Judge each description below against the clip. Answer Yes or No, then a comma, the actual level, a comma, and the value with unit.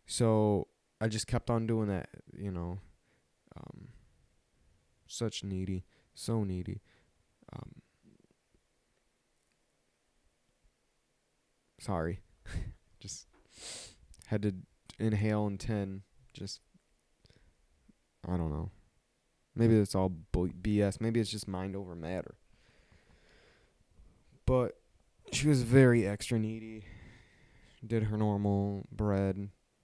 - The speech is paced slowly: Yes, slow, 95 wpm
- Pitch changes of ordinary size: Yes, average, 3.2 semitones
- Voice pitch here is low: Yes, low, 100 Hz